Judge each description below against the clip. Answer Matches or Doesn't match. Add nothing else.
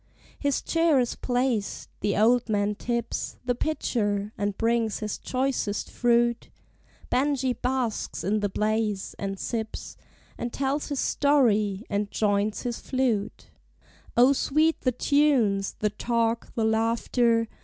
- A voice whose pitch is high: Matches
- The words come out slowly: Matches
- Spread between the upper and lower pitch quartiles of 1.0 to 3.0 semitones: Doesn't match